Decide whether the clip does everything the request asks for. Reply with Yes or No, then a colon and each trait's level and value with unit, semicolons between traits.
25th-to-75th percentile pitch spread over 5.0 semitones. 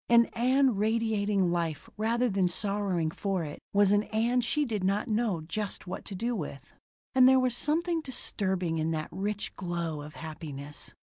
Yes: wide, 5.4 semitones